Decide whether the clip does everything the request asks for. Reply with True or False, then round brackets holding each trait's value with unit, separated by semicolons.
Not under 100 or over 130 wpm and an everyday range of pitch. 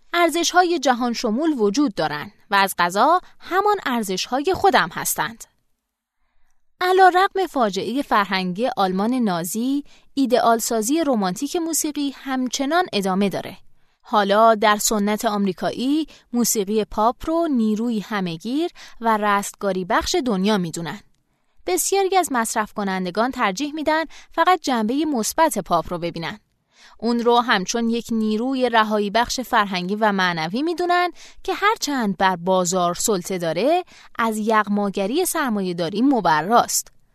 False (125 wpm; 7.2 semitones)